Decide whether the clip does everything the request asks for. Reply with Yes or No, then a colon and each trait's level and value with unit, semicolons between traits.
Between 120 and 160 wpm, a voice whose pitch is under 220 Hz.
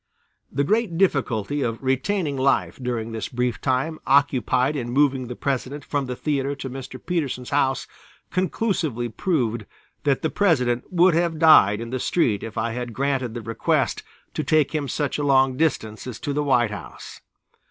No: average, 175 wpm; low, 135 Hz